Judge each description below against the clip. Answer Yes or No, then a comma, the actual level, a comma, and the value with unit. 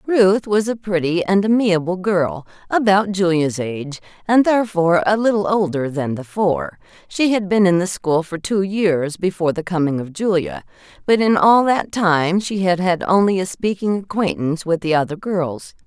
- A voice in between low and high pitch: Yes, medium, 180 Hz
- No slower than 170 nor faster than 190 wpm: Yes, average, 180 wpm